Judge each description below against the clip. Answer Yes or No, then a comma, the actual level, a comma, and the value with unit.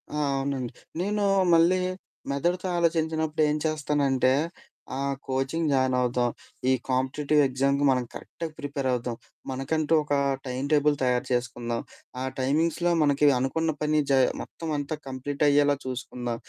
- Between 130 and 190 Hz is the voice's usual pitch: Yes, medium, 140 Hz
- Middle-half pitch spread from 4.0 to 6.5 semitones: No, average, 3.2 semitones